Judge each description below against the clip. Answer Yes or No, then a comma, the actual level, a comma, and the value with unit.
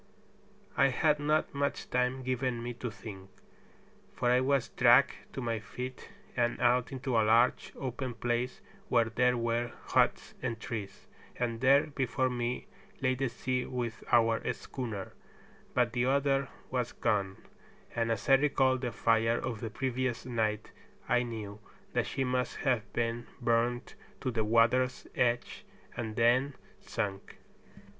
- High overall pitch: No, low, 120 Hz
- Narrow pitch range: Yes, narrow, 2.0 semitones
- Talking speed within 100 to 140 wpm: No, average, 150 wpm